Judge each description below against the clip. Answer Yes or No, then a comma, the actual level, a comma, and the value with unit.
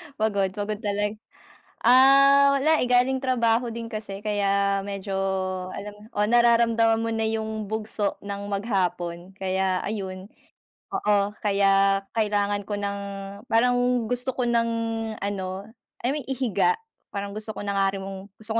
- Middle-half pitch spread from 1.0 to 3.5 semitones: Yes, average, 2.8 semitones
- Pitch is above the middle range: Yes, high, 210 Hz